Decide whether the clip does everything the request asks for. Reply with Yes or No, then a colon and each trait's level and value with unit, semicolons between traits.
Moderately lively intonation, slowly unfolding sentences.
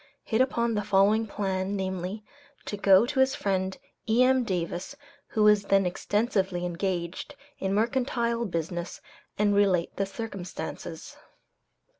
Yes: average, 3.2 semitones; slow, 125 wpm